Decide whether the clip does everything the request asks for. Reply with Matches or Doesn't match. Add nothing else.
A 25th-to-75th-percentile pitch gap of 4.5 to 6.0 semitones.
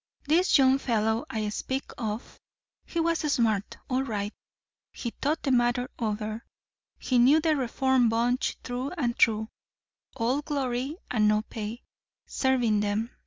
Doesn't match